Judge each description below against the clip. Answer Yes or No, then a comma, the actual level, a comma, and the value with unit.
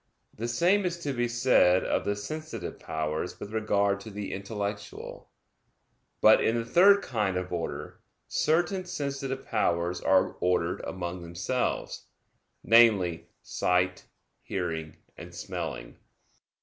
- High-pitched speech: No, low, 100 Hz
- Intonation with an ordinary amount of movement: No, wide, 6.2 semitones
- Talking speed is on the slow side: Yes, slow, 125 wpm